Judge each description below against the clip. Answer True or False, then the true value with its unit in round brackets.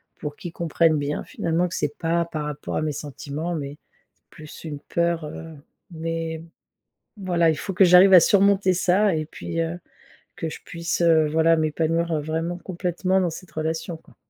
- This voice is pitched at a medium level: True (165 Hz)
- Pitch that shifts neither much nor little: False (2.0 semitones)